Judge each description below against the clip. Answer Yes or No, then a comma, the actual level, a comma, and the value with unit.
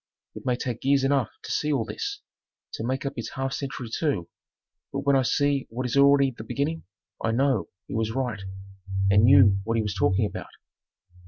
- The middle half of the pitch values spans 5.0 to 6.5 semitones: No, average, 3.8 semitones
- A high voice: No, low, 130 Hz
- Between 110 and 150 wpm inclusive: No, average, 195 wpm